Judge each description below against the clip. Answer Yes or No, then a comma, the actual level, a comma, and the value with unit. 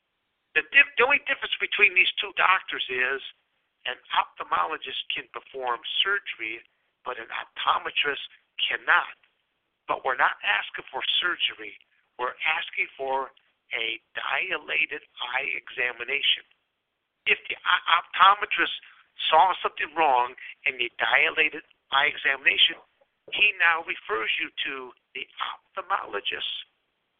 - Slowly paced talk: Yes, slow, 115 wpm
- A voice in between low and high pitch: Yes, medium, 175 Hz